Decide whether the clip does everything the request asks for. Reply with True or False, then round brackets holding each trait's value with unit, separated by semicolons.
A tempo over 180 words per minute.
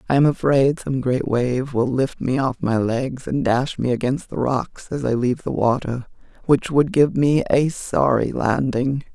True (190 wpm)